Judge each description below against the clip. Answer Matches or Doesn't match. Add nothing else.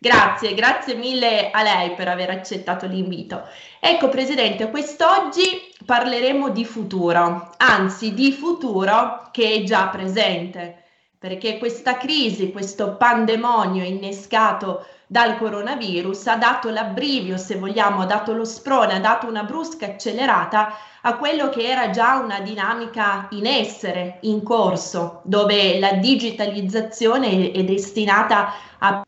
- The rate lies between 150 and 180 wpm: Doesn't match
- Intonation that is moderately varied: Matches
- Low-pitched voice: Doesn't match